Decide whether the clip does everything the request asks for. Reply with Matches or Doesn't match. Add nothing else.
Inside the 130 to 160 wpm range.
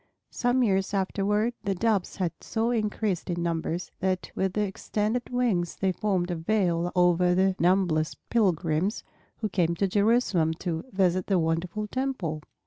Matches